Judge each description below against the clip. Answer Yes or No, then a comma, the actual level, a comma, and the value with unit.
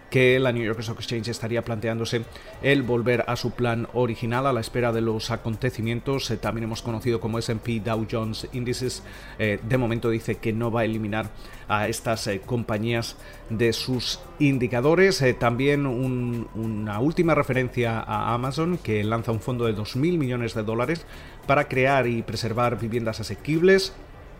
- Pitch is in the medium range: No, low, 115 Hz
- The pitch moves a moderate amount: No, narrow, 2.1 semitones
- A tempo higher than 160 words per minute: No, average, 155 wpm